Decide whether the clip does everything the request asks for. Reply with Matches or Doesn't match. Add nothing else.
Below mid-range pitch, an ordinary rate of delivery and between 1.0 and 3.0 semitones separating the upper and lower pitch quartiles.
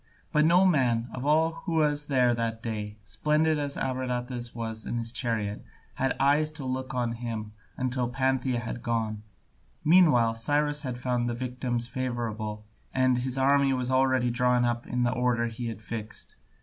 Matches